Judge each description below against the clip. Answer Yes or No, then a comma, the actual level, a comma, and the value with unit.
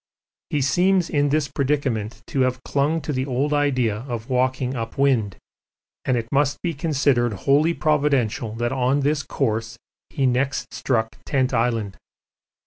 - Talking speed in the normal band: Yes, average, 150 wpm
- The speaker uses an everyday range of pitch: Yes, average, 3.3 semitones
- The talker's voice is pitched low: Yes, low, 130 Hz